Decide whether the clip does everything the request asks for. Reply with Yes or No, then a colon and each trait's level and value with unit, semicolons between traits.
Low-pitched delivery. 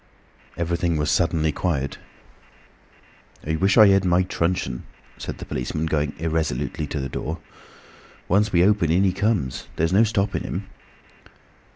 Yes: very low, 85 Hz